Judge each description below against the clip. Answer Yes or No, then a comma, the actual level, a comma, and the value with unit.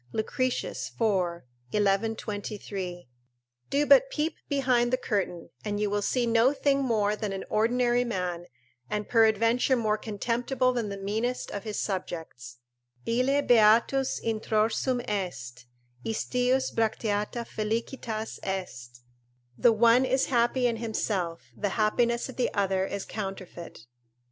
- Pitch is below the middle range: No, high, 220 Hz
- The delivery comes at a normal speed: No, slow, 125 wpm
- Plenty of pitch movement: No, average, 3.7 semitones